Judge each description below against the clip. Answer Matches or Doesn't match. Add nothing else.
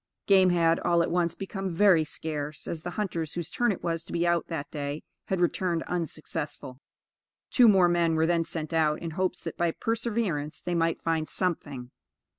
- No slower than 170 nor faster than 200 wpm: Matches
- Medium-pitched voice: Matches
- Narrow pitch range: Matches